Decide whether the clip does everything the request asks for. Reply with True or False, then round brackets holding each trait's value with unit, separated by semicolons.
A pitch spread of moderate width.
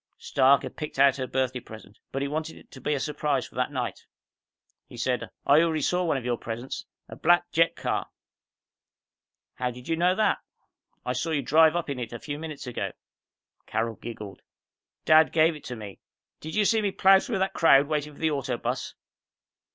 True (4.3 semitones)